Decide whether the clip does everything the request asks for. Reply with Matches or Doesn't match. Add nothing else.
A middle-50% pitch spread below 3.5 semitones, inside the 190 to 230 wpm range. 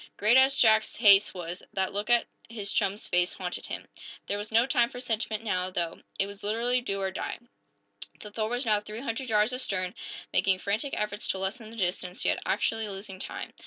Matches